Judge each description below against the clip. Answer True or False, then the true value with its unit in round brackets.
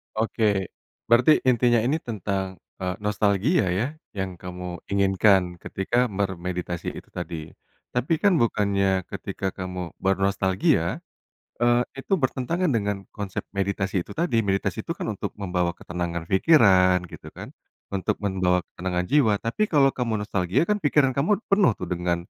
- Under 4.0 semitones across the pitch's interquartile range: False (4.7 semitones)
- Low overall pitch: True (100 Hz)